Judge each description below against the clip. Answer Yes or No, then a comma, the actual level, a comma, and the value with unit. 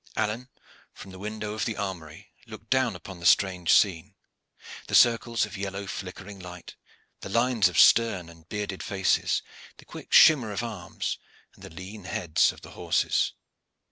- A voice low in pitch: Yes, low, 100 Hz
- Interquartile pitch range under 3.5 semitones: Yes, average, 3.1 semitones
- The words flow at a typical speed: Yes, average, 165 wpm